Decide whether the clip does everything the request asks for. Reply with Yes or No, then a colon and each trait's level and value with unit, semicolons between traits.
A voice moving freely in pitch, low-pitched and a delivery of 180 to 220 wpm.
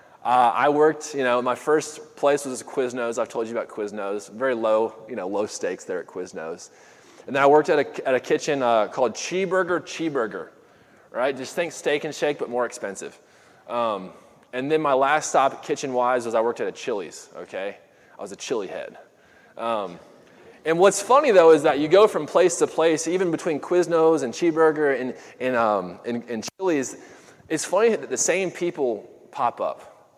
No: wide, 6.3 semitones; medium, 155 Hz; average, 195 wpm